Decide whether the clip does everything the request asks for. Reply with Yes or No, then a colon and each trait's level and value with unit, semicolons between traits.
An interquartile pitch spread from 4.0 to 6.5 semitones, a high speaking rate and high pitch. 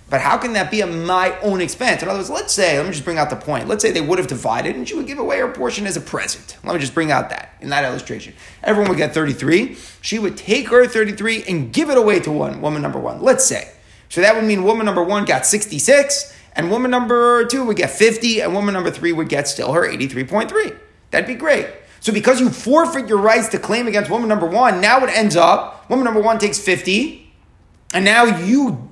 Yes: average, 4.3 semitones; fast, 245 wpm; high, 220 Hz